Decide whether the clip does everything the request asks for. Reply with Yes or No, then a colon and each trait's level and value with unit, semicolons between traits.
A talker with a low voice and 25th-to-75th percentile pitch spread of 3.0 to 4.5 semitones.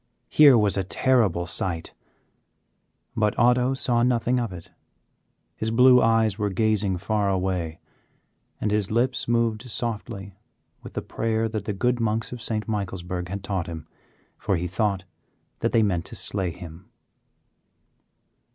Yes: low, 105 Hz; average, 3.5 semitones